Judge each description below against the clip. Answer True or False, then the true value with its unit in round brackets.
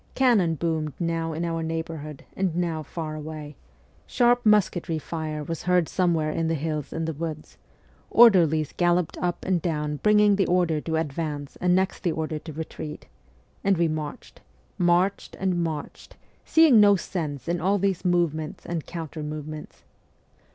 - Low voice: False (165 Hz)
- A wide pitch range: False (2.6 semitones)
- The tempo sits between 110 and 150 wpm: False (160 wpm)